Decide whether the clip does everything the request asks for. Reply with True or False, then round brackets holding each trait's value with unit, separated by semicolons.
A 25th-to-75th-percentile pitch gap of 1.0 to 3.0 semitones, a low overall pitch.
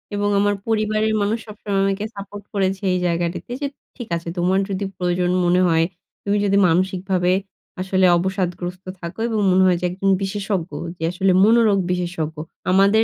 False (2.4 semitones; 190 Hz)